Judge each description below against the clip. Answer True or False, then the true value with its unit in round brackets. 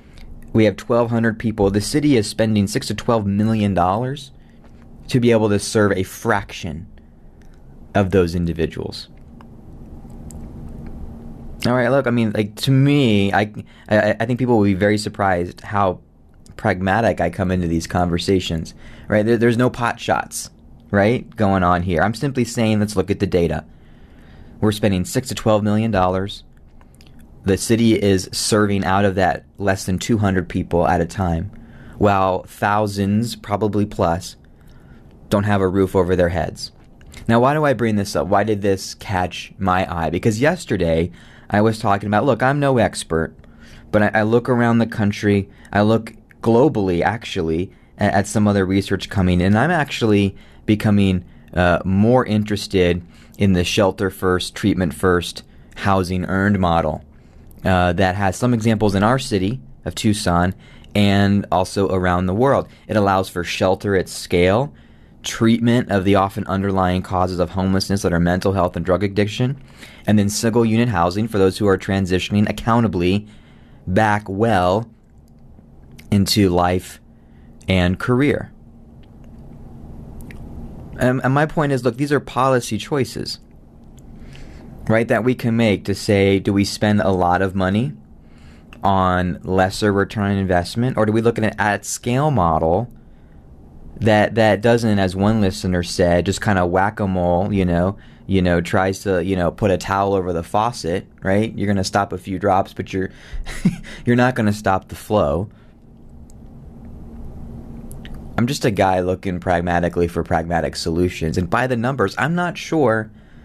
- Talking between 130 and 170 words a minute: True (160 wpm)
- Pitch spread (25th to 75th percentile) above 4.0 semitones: False (3.6 semitones)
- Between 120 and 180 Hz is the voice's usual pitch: False (100 Hz)